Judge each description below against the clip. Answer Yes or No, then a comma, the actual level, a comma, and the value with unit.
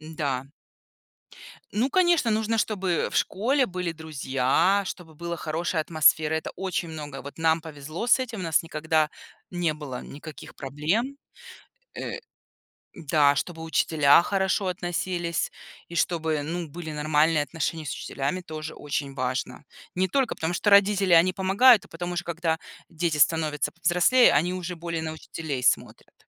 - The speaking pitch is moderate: Yes, medium, 165 Hz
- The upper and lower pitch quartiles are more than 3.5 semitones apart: No, average, 3.2 semitones